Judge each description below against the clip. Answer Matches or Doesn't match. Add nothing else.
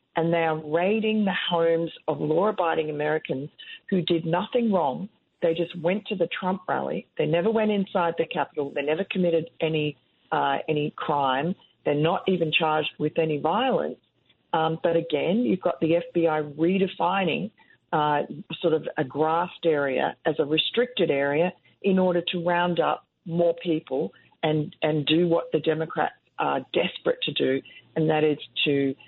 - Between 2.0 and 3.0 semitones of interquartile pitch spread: Matches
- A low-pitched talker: Doesn't match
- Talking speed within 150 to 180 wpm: Matches